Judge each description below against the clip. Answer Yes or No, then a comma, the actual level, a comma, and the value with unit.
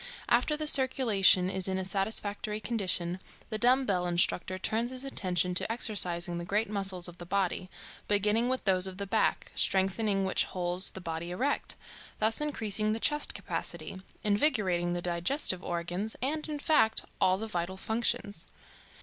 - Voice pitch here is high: Yes, high, 195 Hz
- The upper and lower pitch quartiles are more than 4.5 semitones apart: No, average, 3.8 semitones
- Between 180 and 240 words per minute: No, average, 160 wpm